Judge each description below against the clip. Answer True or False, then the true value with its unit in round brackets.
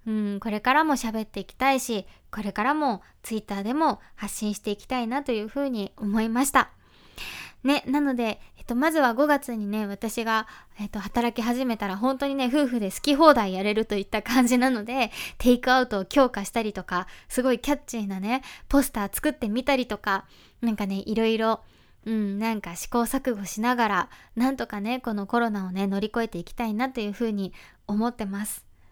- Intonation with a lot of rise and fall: False (3.7 semitones)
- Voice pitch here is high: True (225 Hz)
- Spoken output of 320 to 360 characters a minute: False (380 characters per minute)